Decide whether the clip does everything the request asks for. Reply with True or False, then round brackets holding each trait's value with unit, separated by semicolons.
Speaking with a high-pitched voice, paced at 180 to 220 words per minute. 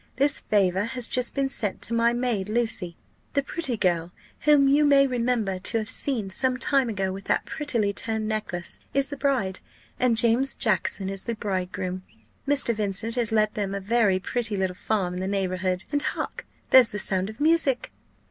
True (220 Hz; 185 wpm)